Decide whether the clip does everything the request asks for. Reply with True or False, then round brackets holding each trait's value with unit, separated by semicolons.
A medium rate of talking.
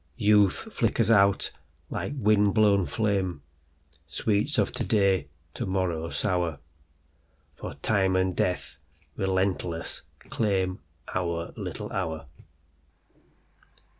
False (85 wpm)